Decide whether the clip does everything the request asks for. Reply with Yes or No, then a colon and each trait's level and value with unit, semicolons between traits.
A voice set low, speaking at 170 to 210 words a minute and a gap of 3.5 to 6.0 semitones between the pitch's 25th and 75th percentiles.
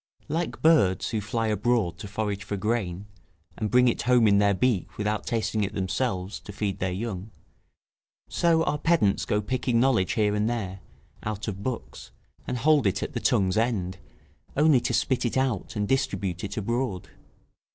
Yes: low, 105 Hz; average, 175 wpm; average, 3.8 semitones